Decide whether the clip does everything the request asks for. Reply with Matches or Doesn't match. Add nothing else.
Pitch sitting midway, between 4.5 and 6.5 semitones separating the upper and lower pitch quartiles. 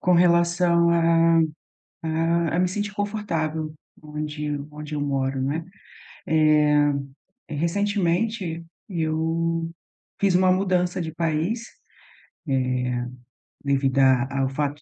Doesn't match